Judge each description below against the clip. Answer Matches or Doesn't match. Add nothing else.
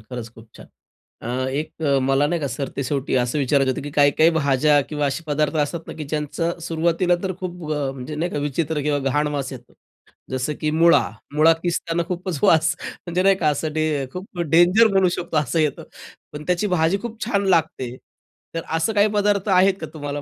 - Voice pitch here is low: Doesn't match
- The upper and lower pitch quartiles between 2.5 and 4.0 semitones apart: Matches